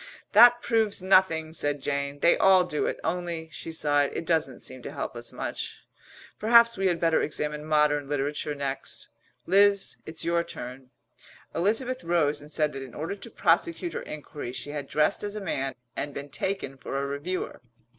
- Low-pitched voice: No, medium, 155 Hz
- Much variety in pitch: No, average, 4.8 semitones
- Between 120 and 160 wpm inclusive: No, average, 180 wpm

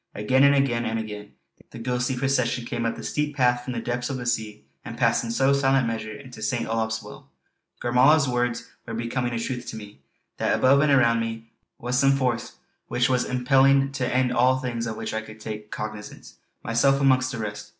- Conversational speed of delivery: No, fast, 210 wpm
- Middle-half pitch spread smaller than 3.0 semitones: Yes, narrow, 2.5 semitones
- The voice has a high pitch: No, low, 125 Hz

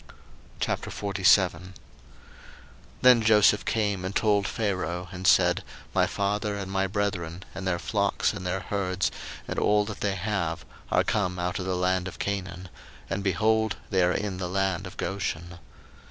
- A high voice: No, very low, 95 Hz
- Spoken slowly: No, average, 155 wpm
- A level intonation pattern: Yes, narrow, 2.1 semitones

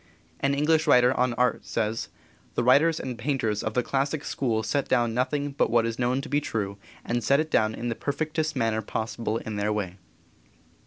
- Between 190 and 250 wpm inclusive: Yes, average, 200 wpm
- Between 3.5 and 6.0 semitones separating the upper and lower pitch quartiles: Yes, average, 4.0 semitones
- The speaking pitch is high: No, low, 125 Hz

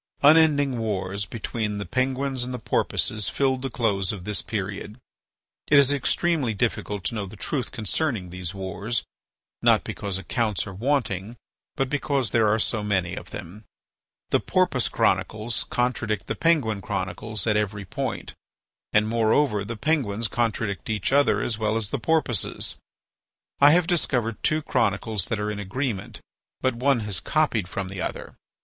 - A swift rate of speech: No, average, 160 wpm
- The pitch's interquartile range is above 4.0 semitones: Yes, average, 4.4 semitones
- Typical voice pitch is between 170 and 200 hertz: No, low, 110 Hz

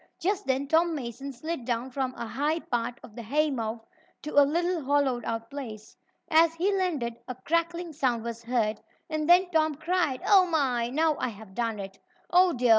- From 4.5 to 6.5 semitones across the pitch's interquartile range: Yes, wide, 5.6 semitones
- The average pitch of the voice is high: Yes, very high, 275 Hz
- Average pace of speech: Yes, average, 190 wpm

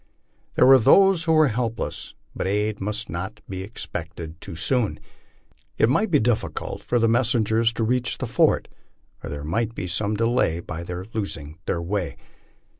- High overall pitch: No, low, 110 Hz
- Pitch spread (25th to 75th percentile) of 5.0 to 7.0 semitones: Yes, wide, 5.4 semitones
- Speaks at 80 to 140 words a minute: No, average, 170 wpm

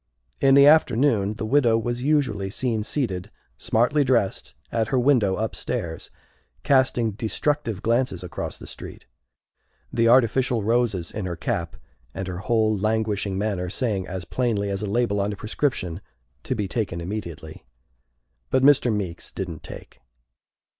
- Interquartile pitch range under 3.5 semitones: No, average, 4.2 semitones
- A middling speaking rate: Yes, average, 145 wpm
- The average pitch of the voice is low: Yes, low, 110 Hz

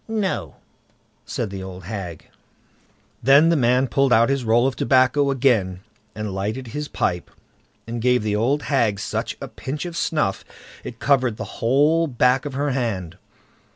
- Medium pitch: No, low, 125 Hz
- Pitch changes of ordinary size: Yes, average, 4.5 semitones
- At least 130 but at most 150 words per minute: No, average, 160 wpm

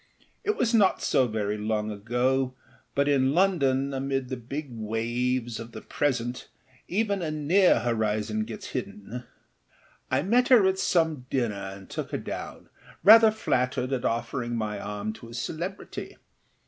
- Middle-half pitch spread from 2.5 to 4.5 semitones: No, wide, 5.4 semitones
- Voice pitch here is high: No, low, 125 Hz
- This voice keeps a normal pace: Yes, average, 150 wpm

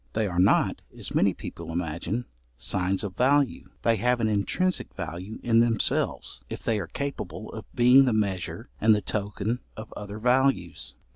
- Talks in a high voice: No, low, 110 Hz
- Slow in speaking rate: No, average, 165 wpm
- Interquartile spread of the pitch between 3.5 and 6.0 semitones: Yes, average, 4.1 semitones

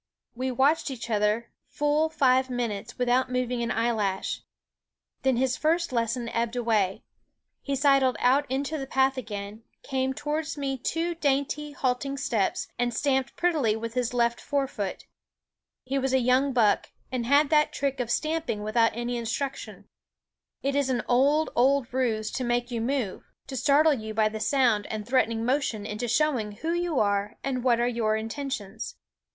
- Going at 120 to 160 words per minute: No, average, 170 wpm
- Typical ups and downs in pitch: Yes, average, 3.3 semitones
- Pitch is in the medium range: No, very high, 255 Hz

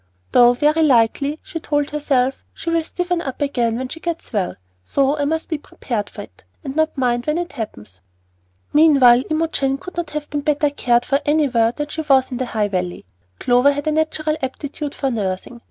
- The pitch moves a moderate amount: Yes, average, 4.0 semitones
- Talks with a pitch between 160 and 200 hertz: No, very high, 280 Hz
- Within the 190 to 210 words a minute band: Yes, average, 200 wpm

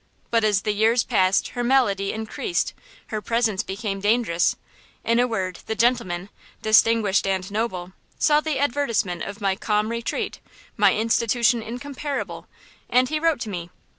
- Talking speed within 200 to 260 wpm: No, average, 150 wpm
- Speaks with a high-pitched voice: Yes, high, 220 Hz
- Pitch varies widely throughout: No, average, 3.6 semitones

